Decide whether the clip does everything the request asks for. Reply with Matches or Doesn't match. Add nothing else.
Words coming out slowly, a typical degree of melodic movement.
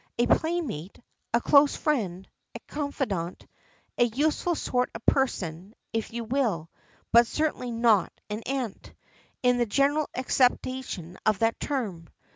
Matches